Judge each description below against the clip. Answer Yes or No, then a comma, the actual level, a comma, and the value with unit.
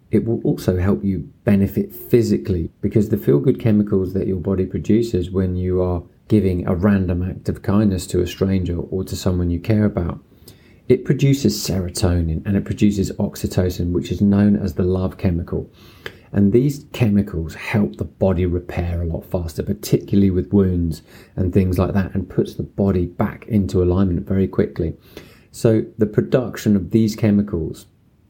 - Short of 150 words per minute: No, average, 170 wpm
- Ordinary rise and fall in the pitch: No, narrow, 2.3 semitones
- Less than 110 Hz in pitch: Yes, very low, 95 Hz